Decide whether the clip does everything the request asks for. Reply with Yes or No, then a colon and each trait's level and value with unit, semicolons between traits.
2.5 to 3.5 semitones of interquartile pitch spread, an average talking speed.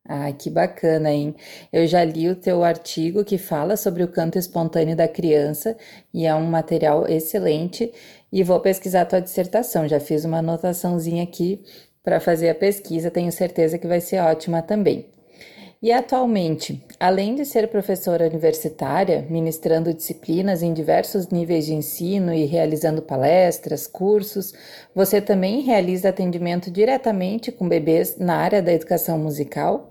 Yes: average, 3.0 semitones; average, 150 wpm